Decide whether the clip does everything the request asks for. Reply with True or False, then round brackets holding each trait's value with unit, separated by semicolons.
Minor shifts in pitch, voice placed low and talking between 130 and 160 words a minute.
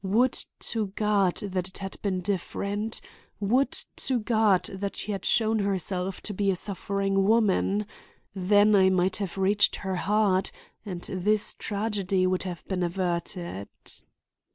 False (2.1 semitones; 195 Hz; 145 wpm)